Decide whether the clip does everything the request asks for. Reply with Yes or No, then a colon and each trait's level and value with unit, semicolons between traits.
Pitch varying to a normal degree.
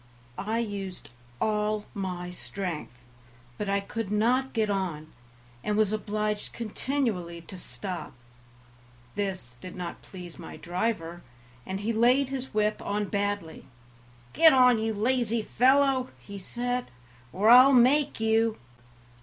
Yes: average, 4.1 semitones